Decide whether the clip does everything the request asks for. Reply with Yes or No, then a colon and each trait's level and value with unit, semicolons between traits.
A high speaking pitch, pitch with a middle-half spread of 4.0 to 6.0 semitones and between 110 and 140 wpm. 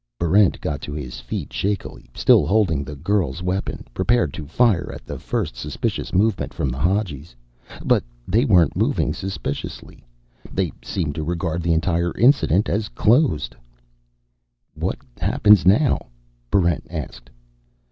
No: very low, 90 Hz; average, 4.9 semitones; slow, 135 wpm